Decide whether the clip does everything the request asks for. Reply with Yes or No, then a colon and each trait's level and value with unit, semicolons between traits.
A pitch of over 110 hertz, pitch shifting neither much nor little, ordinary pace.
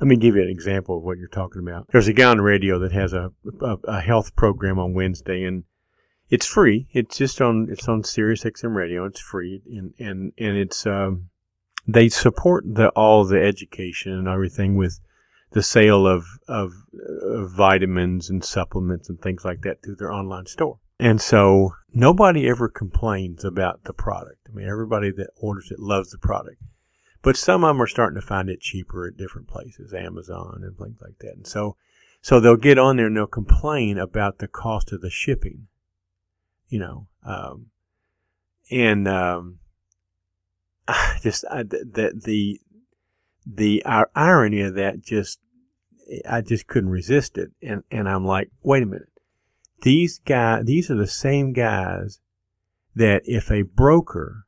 No: low, 100 Hz; average, 3.5 semitones; average, 175 wpm